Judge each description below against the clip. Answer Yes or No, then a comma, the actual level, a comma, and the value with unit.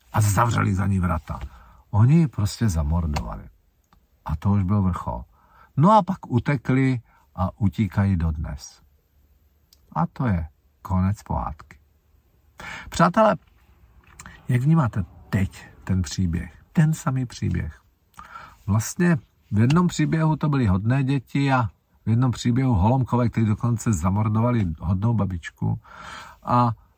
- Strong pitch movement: Yes, wide, 6.7 semitones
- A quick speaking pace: No, average, 120 wpm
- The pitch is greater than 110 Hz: No, low, 105 Hz